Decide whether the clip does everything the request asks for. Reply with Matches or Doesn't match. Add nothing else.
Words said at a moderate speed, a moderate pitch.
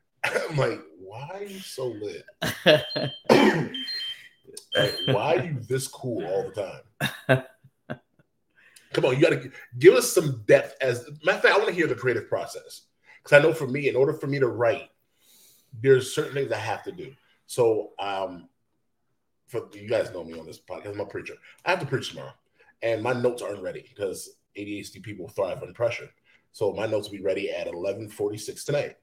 Matches